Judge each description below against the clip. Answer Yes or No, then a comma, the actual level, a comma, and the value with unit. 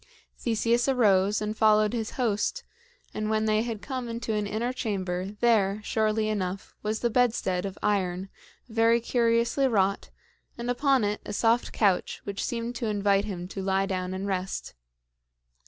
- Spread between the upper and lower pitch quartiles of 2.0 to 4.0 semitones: Yes, average, 2.9 semitones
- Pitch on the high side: Yes, high, 215 Hz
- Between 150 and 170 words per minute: Yes, average, 160 wpm